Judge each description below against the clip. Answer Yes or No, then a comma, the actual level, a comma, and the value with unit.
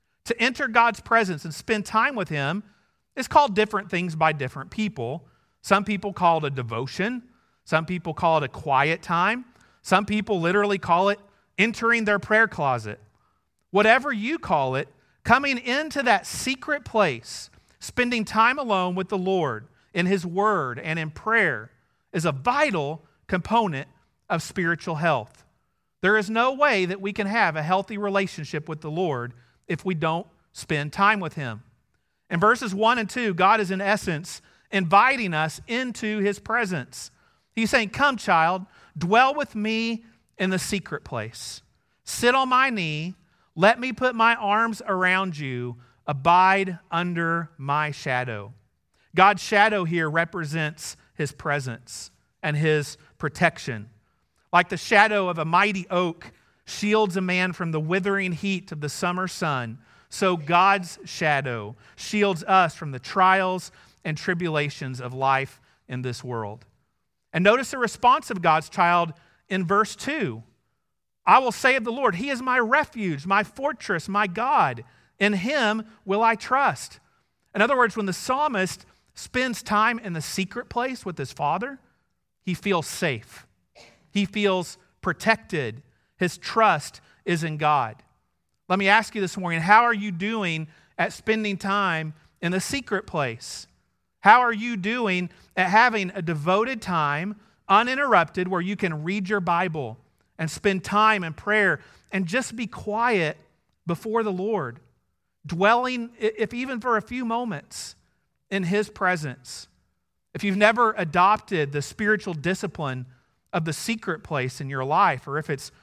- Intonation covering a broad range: Yes, wide, 5.7 semitones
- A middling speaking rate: Yes, average, 155 wpm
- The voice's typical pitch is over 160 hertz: Yes, medium, 185 Hz